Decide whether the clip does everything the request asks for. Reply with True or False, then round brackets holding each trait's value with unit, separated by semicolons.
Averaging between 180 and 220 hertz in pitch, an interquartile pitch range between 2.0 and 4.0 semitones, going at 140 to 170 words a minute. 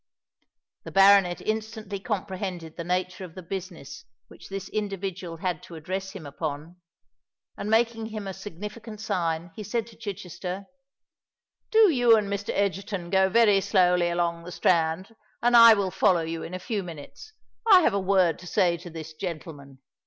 True (190 Hz; 3.3 semitones; 165 wpm)